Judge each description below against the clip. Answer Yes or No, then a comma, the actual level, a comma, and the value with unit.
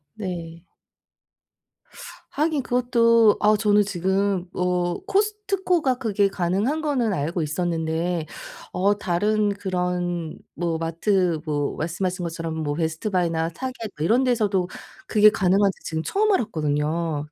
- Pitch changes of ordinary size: Yes, average, 4.6 semitones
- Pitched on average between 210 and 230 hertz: No, medium, 185 Hz